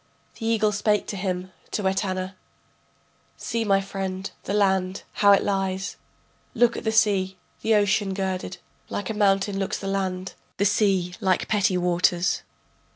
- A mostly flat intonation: Yes, narrow, 1.6 semitones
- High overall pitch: Yes, high, 195 Hz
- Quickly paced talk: No, average, 155 wpm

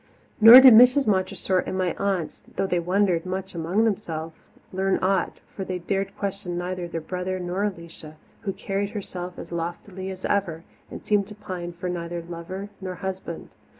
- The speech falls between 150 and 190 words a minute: Yes, average, 175 wpm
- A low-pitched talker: No, medium, 185 Hz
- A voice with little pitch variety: Yes, narrow, 2.3 semitones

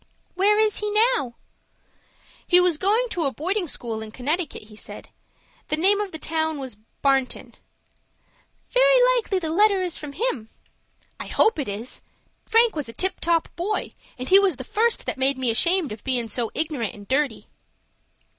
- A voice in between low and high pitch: No, very high, 320 Hz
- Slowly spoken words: No, average, 175 wpm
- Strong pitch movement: Yes, wide, 7.5 semitones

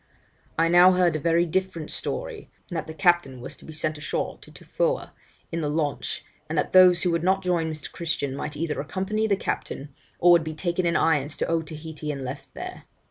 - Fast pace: Yes, fast, 210 wpm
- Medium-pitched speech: Yes, medium, 165 Hz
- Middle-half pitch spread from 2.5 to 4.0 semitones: Yes, average, 2.8 semitones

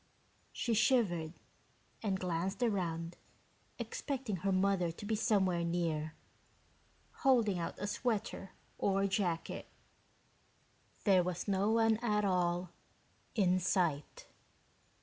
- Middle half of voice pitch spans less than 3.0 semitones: No, average, 3.5 semitones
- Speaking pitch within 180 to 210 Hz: Yes, high, 190 Hz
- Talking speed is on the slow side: Yes, slow, 105 wpm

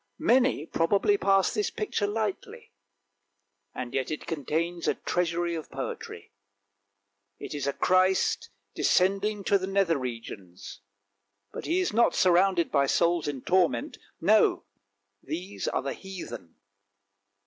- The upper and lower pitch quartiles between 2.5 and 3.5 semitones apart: No, average, 5.0 semitones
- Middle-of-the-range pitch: Yes, medium, 175 Hz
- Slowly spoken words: Yes, slow, 125 wpm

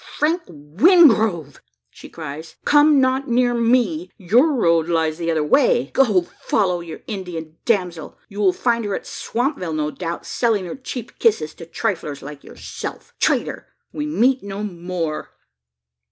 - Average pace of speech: Yes, average, 150 wpm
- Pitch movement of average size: No, wide, 6.9 semitones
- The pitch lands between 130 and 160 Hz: No, high, 195 Hz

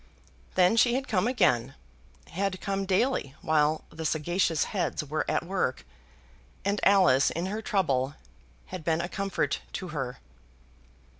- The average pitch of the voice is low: No, medium, 180 Hz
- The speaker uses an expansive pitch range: No, average, 4.3 semitones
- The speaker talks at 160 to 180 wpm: No, average, 140 wpm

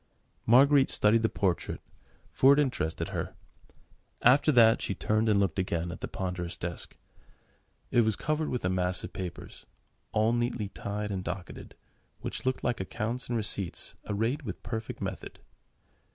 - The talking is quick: No, average, 155 wpm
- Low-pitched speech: Yes, low, 110 Hz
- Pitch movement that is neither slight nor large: Yes, average, 4.7 semitones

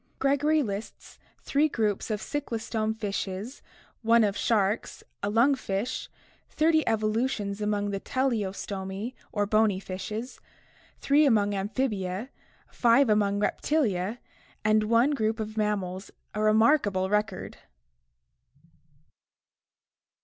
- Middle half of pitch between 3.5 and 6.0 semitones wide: No, average, 3.1 semitones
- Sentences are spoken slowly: Yes, slow, 105 wpm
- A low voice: No, high, 215 Hz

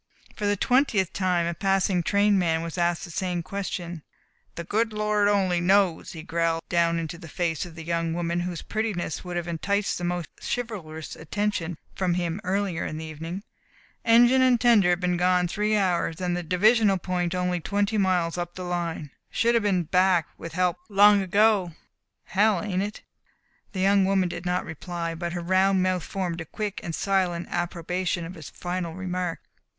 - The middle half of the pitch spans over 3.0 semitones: No, average, 2.7 semitones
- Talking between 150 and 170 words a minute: No, average, 185 wpm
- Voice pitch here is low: No, medium, 180 Hz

